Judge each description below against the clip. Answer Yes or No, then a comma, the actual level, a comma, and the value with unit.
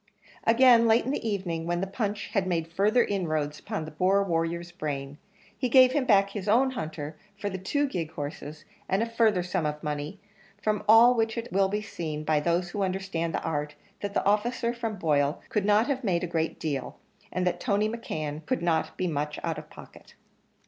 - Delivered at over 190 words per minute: Yes, fast, 205 wpm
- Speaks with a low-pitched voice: No, medium, 185 Hz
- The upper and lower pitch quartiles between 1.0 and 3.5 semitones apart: No, average, 5.3 semitones